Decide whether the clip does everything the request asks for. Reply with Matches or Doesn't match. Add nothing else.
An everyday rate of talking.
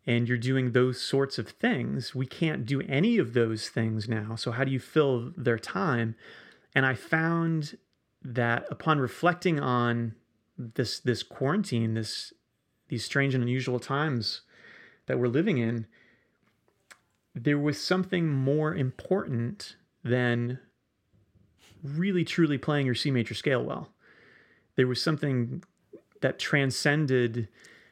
Doesn't match